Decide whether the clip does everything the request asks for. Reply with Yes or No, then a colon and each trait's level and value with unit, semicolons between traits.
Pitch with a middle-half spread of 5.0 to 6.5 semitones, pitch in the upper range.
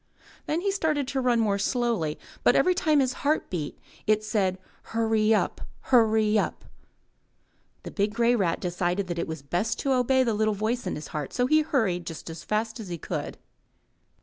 Yes: wide, 5.4 semitones; high, 220 Hz